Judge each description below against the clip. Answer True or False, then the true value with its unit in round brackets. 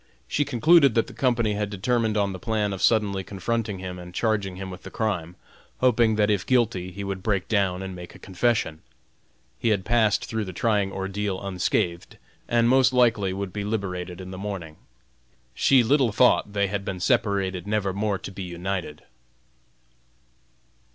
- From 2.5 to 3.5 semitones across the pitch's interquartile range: True (3.2 semitones)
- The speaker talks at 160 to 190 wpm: True (175 wpm)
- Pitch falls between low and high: False (100 Hz)